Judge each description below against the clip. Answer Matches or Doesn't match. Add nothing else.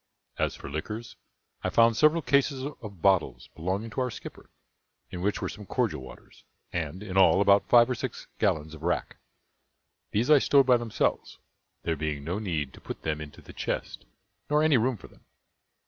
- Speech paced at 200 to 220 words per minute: Doesn't match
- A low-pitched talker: Matches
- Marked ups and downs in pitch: Matches